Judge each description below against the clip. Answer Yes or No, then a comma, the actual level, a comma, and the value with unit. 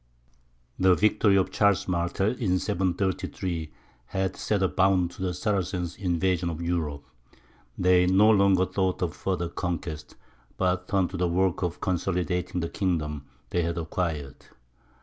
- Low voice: Yes, very low, 90 Hz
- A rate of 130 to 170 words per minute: Yes, average, 145 wpm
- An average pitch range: No, narrow, 1.8 semitones